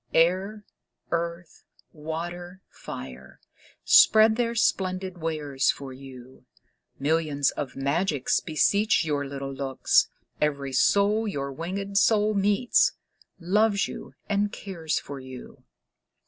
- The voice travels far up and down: Yes, wide, 6.0 semitones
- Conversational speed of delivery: No, slow, 105 wpm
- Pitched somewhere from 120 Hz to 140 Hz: No, medium, 170 Hz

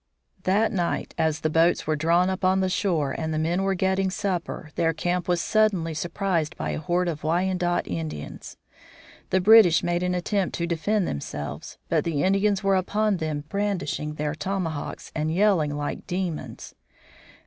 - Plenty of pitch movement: No, average, 3.2 semitones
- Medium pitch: Yes, medium, 175 Hz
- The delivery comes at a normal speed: Yes, average, 170 wpm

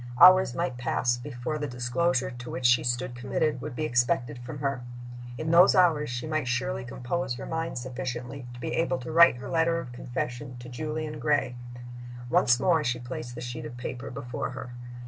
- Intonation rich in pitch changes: No, average, 3.9 semitones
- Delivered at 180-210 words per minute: Yes, average, 190 wpm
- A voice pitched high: No, low, 130 Hz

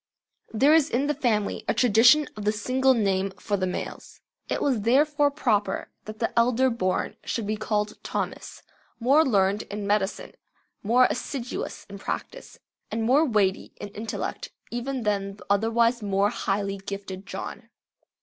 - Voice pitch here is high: Yes, high, 220 Hz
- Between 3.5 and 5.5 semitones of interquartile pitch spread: Yes, average, 4.0 semitones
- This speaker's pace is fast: No, average, 155 wpm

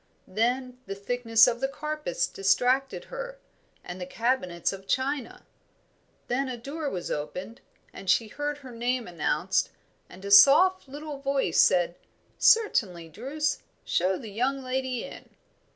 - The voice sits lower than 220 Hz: No, high, 245 Hz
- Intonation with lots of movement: Yes, wide, 6.0 semitones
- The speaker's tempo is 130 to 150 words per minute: Yes, average, 140 wpm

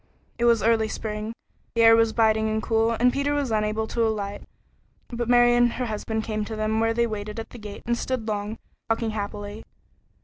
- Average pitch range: No, narrow, 1.5 semitones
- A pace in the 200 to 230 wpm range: Yes, fast, 205 wpm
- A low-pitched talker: No, high, 220 Hz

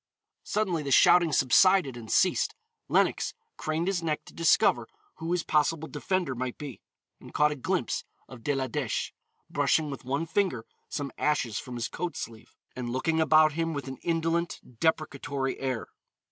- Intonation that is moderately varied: Yes, average, 4.0 semitones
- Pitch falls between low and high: Yes, medium, 150 Hz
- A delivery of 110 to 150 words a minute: No, average, 170 wpm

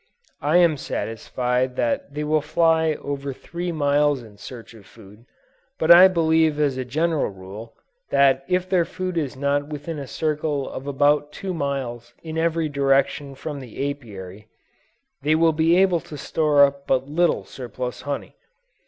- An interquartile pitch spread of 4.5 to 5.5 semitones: No, average, 3.6 semitones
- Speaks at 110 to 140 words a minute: No, average, 160 wpm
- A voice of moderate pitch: Yes, medium, 145 Hz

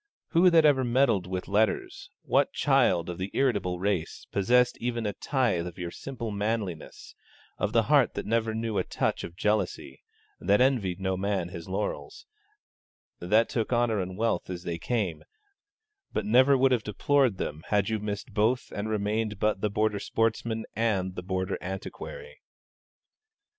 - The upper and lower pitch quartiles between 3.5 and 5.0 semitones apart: Yes, average, 3.9 semitones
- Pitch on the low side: Yes, low, 105 Hz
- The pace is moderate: Yes, average, 165 wpm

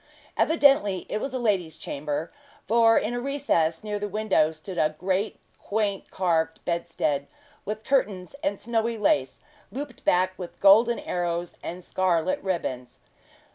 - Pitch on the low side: No, high, 195 Hz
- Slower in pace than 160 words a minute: Yes, average, 140 wpm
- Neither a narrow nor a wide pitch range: Yes, average, 4.8 semitones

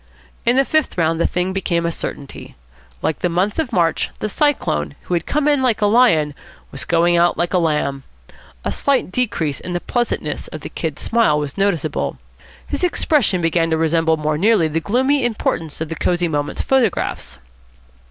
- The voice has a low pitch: No, medium, 175 Hz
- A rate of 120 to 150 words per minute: No, average, 185 wpm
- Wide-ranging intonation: Yes, wide, 6.3 semitones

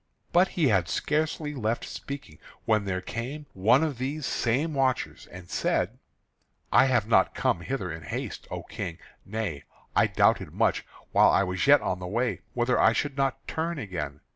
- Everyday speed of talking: Yes, average, 175 wpm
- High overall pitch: No, low, 120 Hz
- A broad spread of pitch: Yes, wide, 7.0 semitones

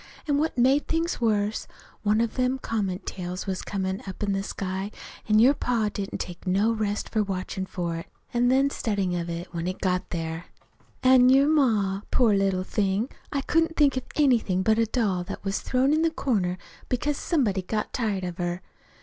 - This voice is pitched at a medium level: No, high, 210 Hz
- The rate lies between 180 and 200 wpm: Yes, average, 195 wpm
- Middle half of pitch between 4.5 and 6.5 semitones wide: Yes, average, 5.2 semitones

